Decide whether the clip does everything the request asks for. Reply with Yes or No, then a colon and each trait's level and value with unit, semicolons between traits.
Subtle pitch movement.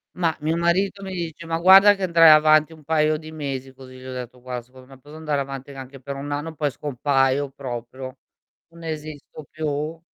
No: average, 3.4 semitones